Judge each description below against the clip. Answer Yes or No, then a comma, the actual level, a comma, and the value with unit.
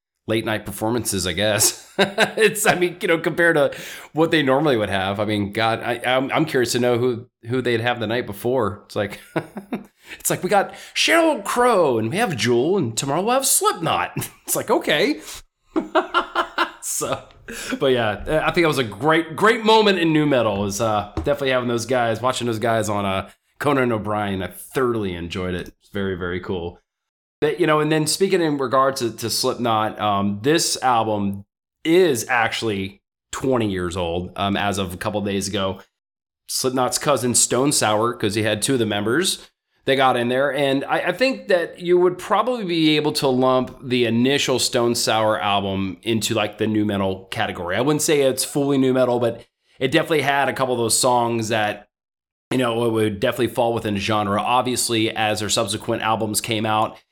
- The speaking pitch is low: Yes, low, 120 Hz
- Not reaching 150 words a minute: No, average, 195 wpm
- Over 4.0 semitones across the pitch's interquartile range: Yes, average, 4.9 semitones